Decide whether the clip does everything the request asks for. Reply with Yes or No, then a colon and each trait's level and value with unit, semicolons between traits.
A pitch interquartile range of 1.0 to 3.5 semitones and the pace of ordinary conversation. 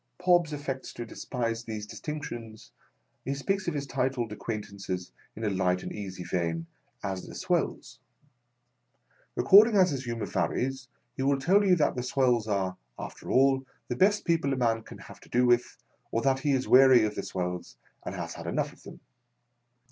No: average, 4.7 semitones; average, 185 wpm